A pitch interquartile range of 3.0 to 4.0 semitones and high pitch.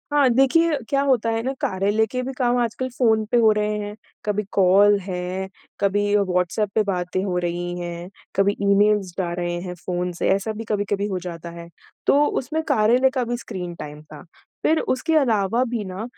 No: average, 4.6 semitones; high, 205 Hz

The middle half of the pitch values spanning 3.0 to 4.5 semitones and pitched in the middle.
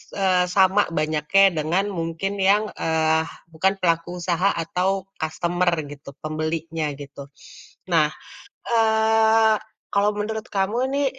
Yes: average, 4.1 semitones; medium, 180 Hz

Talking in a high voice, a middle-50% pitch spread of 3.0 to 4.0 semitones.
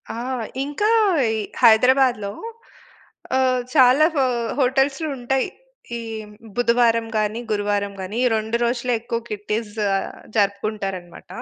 Yes: high, 235 Hz; average, 3.6 semitones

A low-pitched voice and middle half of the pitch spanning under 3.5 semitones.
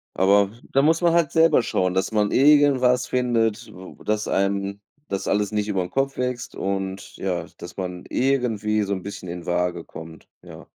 No: low, 105 Hz; average, 5.0 semitones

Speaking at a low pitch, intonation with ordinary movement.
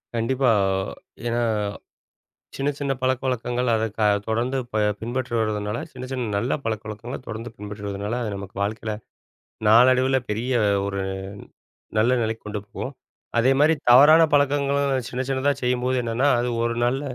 Yes: low, 120 Hz; average, 3.1 semitones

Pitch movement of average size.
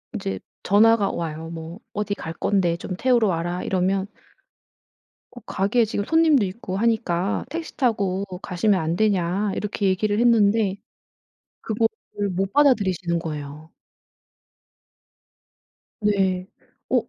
Yes: average, 3.7 semitones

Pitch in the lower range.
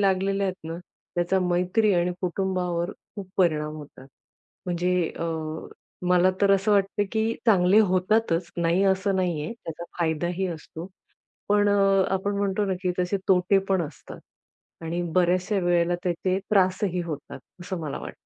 No: medium, 185 Hz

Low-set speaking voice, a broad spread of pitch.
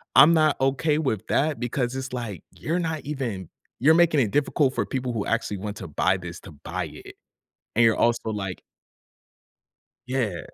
Yes: low, 125 Hz; wide, 6.0 semitones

